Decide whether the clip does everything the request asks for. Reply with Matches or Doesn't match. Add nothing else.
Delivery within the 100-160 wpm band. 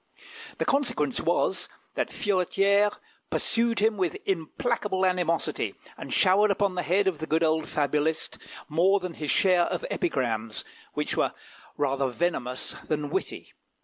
Matches